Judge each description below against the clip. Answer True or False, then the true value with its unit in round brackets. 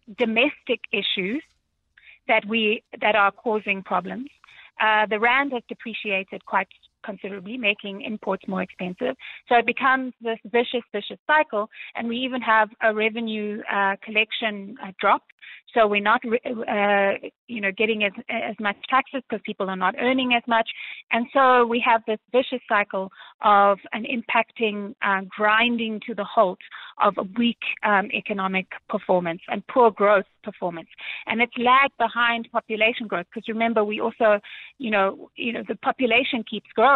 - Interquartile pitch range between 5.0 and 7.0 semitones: False (2.8 semitones)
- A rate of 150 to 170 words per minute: True (160 wpm)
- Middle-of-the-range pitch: False (220 Hz)